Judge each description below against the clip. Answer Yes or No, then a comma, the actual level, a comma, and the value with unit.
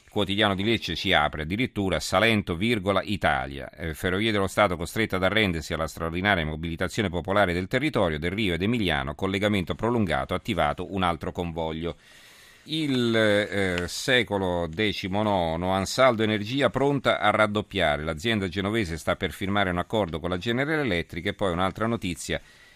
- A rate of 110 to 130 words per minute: No, average, 150 wpm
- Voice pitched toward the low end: Yes, very low, 95 Hz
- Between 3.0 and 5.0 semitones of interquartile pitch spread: Yes, average, 3.7 semitones